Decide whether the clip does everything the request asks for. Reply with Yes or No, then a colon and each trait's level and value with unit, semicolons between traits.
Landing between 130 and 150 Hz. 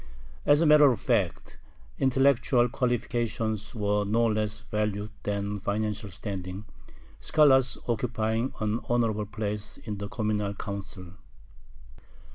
No: low, 110 Hz